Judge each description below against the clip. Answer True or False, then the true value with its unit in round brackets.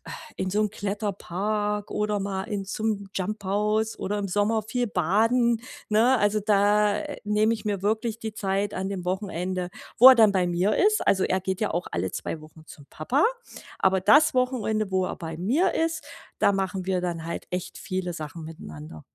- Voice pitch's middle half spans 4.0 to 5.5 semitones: False (2.7 semitones)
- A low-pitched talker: False (200 Hz)